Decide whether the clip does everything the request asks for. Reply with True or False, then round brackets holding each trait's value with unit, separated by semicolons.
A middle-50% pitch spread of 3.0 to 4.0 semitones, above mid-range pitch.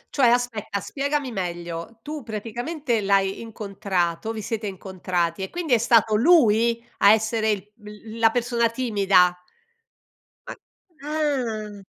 True (3.5 semitones; 220 Hz)